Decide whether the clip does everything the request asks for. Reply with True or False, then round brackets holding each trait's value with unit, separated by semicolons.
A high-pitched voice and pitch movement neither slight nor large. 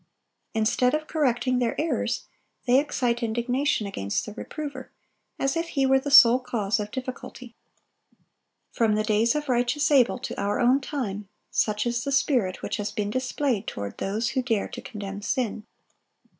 True (240 Hz; 4.1 semitones)